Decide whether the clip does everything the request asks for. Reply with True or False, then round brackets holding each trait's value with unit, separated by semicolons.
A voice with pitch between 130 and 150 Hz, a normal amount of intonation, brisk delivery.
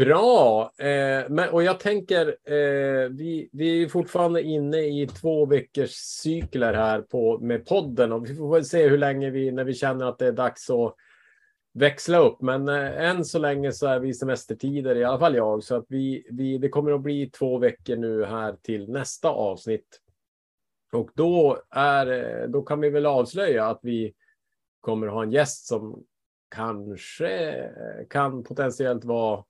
False (135 Hz; 3.7 semitones; 175 wpm)